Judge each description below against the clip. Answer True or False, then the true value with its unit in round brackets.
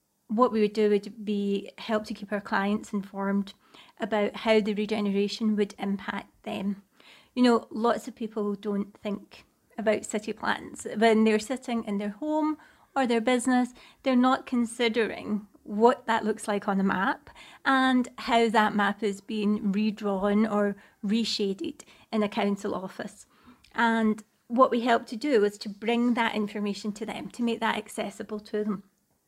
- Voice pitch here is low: False (215 Hz)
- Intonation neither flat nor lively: False (2.2 semitones)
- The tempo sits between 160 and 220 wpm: True (165 wpm)